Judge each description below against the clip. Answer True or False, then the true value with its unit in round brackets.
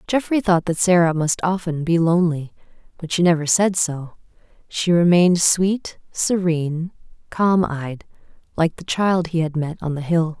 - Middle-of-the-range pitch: True (170 Hz)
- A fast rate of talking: False (160 wpm)